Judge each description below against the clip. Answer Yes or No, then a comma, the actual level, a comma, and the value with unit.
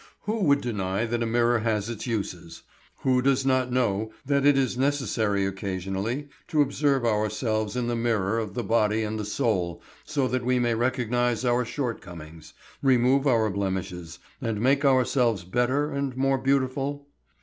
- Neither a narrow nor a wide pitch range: Yes, average, 3.8 semitones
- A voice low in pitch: Yes, low, 120 Hz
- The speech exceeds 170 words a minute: No, average, 160 wpm